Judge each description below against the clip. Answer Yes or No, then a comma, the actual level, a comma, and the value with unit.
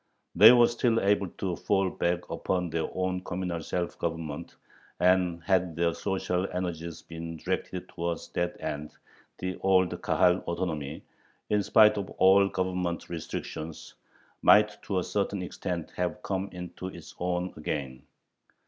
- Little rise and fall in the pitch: Yes, narrow, 2.0 semitones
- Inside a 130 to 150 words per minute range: Yes, average, 140 wpm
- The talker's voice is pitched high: No, very low, 90 Hz